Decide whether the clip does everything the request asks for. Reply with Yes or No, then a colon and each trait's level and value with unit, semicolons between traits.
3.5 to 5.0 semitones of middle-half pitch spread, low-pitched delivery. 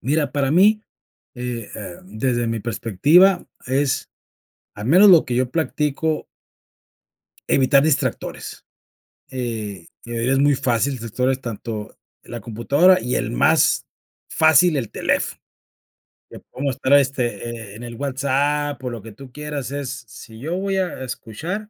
Yes: average, 4.0 semitones; low, 130 Hz